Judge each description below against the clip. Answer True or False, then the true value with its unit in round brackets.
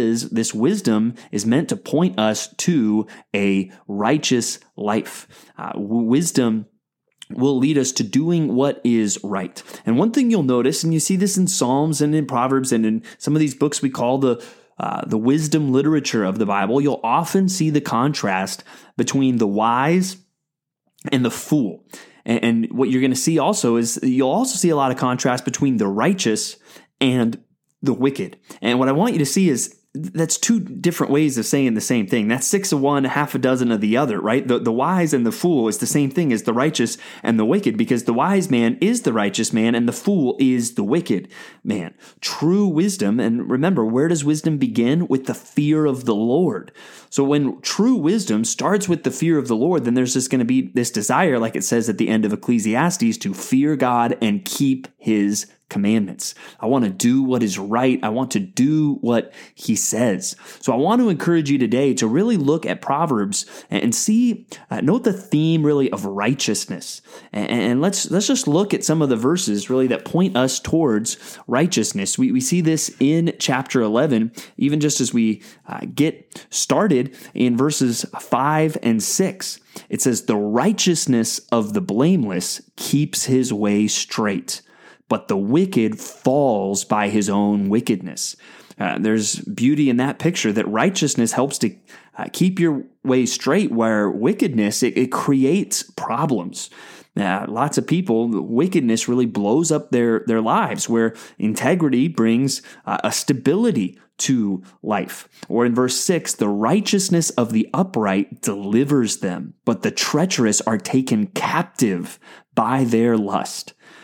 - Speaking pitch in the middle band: False (130 Hz)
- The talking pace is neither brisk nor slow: True (180 wpm)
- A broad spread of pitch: True (5.8 semitones)